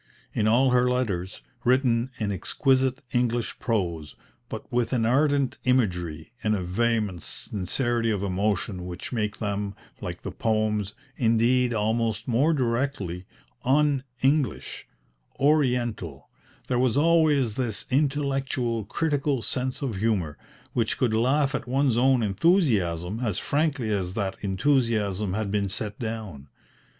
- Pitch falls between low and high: No, low, 115 Hz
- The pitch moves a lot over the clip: No, average, 4.4 semitones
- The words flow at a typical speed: No, slow, 130 wpm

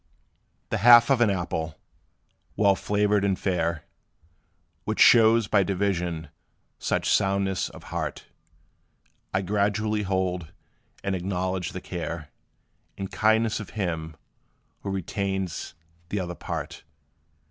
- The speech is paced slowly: Yes, slow, 115 wpm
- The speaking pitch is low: Yes, very low, 95 Hz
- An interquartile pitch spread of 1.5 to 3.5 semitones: Yes, average, 2.7 semitones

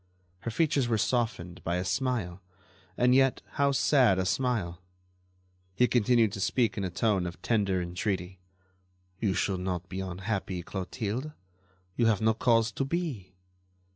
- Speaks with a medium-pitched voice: No, low, 105 Hz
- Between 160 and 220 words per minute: No, average, 150 wpm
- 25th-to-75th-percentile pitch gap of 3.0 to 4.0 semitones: No, average, 4.9 semitones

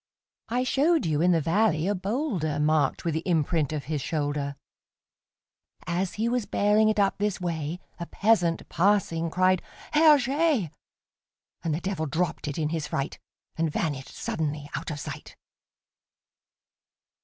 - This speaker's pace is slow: Yes, slow, 130 wpm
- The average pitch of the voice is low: No, medium, 170 Hz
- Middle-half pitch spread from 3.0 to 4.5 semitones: No, average, 5.1 semitones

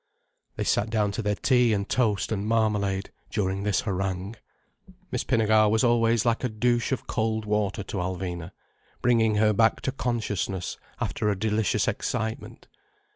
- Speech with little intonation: Yes, narrow, 2.3 semitones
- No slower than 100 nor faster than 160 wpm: Yes, average, 155 wpm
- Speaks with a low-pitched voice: Yes, low, 110 Hz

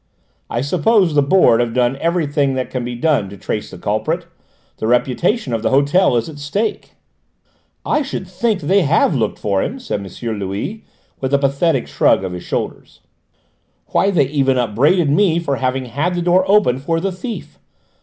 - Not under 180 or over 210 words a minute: Yes, average, 185 wpm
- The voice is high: No, medium, 145 Hz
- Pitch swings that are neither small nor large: No, wide, 6.5 semitones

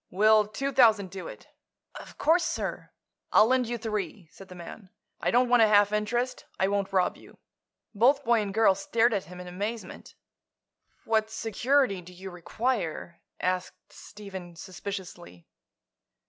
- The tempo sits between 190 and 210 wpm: No, average, 155 wpm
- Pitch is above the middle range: Yes, high, 205 Hz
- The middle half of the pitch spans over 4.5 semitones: No, average, 3.8 semitones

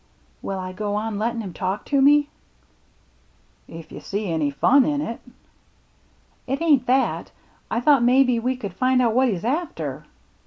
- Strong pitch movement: No, average, 4.9 semitones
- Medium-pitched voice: No, high, 235 Hz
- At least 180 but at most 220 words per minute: Yes, average, 195 wpm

